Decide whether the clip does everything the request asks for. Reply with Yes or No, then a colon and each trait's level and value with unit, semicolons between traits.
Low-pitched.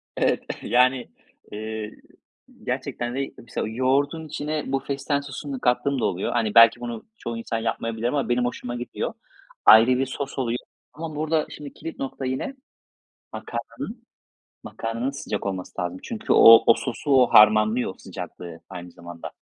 Yes: low, 120 Hz